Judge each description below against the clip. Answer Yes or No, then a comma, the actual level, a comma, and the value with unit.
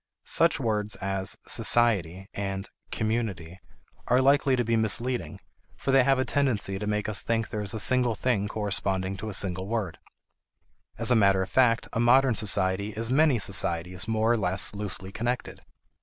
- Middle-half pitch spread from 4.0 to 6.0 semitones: No, average, 3.6 semitones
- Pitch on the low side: Yes, low, 105 Hz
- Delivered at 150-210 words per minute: Yes, average, 170 wpm